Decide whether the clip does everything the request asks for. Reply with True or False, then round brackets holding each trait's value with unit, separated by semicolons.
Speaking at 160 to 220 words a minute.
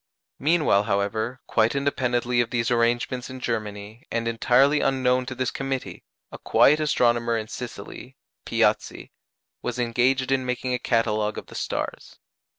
False (145 wpm)